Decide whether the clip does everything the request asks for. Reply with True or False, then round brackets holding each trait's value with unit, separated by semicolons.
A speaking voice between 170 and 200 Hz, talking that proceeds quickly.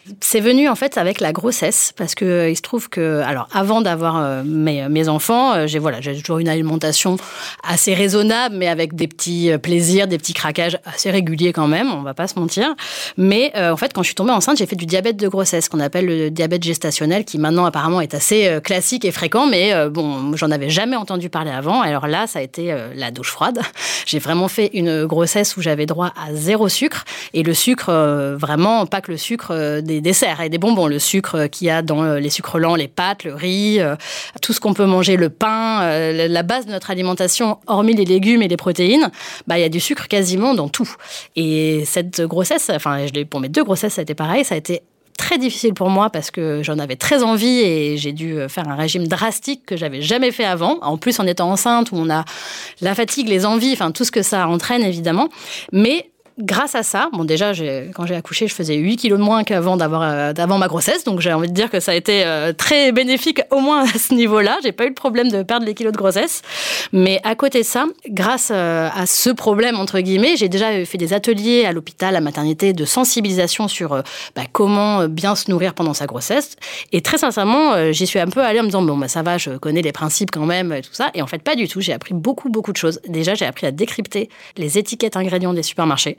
True (185 Hz; 240 wpm)